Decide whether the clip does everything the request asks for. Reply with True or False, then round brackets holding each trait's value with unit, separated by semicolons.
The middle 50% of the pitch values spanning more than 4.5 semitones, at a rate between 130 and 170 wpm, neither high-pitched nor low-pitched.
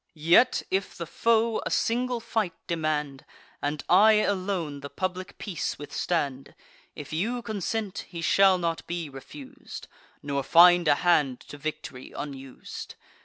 True (5.5 semitones; 135 wpm; 175 Hz)